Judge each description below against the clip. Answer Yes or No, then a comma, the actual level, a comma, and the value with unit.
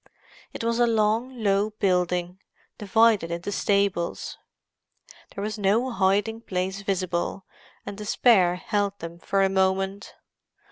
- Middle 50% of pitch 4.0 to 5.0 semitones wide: No, narrow, 2.5 semitones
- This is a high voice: Yes, high, 200 Hz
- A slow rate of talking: Yes, slow, 125 wpm